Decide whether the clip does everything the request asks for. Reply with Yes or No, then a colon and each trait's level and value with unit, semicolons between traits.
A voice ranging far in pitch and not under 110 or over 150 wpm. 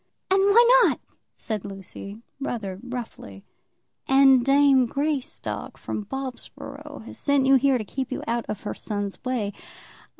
No: average, 4.6 semitones; average, 140 wpm